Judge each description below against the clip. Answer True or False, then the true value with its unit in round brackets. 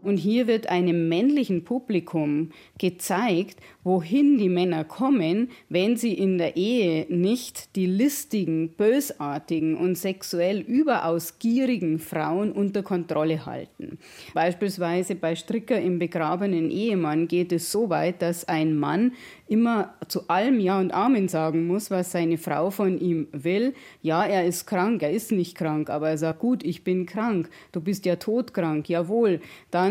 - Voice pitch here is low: False (180 Hz)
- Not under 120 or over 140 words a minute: False (155 wpm)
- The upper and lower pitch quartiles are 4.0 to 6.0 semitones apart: True (4.4 semitones)